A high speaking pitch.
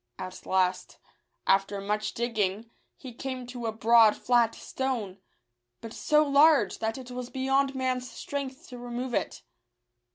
Yes: high, 245 Hz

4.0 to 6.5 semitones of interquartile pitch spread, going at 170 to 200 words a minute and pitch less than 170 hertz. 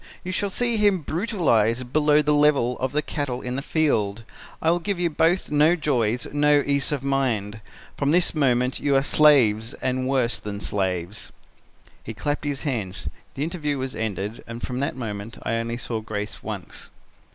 Yes: average, 4.7 semitones; average, 180 wpm; low, 135 Hz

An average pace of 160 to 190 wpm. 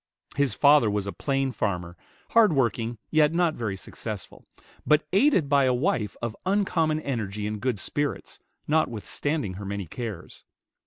No: average, 150 wpm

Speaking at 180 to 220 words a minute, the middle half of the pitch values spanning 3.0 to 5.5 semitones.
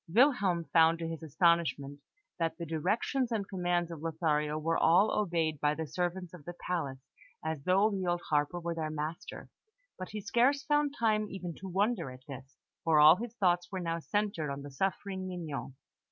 Yes: average, 185 wpm; average, 3.8 semitones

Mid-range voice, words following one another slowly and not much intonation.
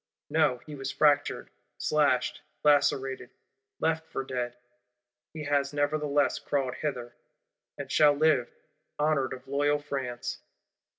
Yes: medium, 145 Hz; slow, 115 wpm; narrow, 2.2 semitones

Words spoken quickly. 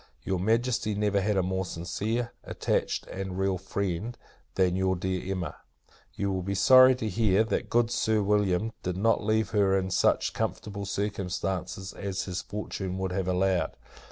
No: average, 165 wpm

